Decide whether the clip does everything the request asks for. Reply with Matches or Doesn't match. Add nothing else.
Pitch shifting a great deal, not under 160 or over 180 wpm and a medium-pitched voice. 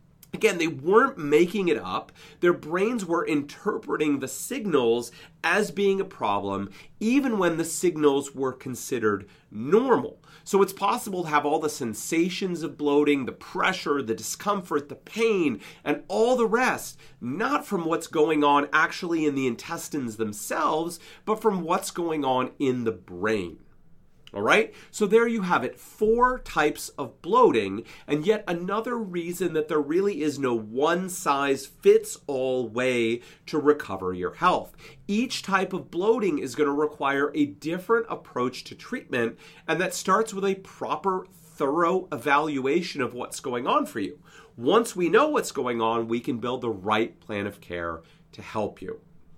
Matches